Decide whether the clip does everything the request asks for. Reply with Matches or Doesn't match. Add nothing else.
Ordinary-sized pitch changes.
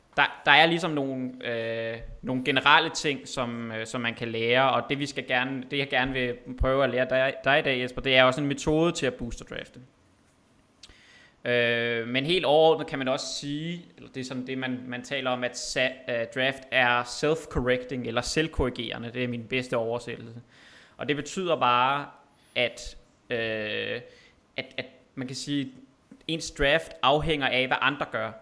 Doesn't match